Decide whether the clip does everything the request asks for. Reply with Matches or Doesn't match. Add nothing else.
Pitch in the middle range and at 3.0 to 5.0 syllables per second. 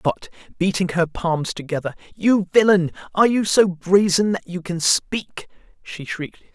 Matches